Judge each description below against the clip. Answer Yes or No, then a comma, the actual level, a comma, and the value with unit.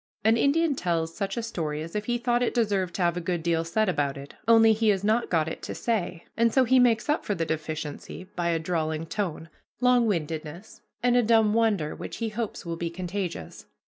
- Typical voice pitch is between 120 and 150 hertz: No, high, 195 Hz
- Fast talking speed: Yes, fast, 225 wpm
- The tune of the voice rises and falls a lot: Yes, wide, 5.7 semitones